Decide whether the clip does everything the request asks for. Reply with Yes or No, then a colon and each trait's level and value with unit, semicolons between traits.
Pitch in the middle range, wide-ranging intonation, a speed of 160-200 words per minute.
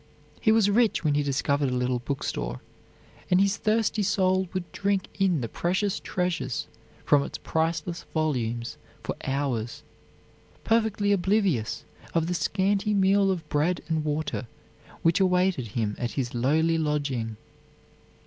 No: medium, 165 Hz; wide, 6.1 semitones; average, 140 wpm